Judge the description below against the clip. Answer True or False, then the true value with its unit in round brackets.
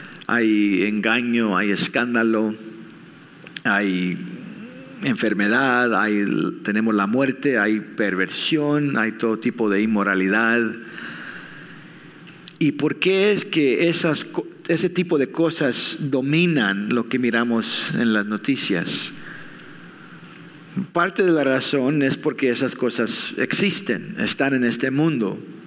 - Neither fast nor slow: False (110 wpm)